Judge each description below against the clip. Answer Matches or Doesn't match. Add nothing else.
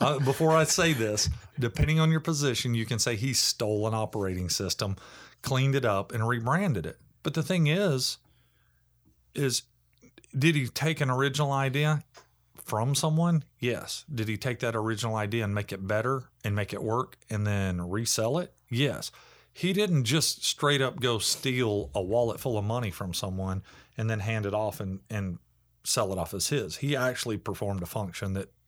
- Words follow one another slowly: Doesn't match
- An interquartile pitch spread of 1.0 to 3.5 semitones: Doesn't match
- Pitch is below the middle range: Matches